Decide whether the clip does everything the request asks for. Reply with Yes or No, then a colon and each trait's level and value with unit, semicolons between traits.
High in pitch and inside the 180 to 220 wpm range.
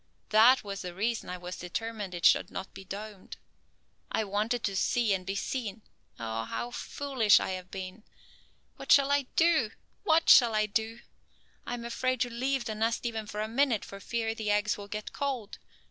Yes: high, 220 Hz; average, 190 wpm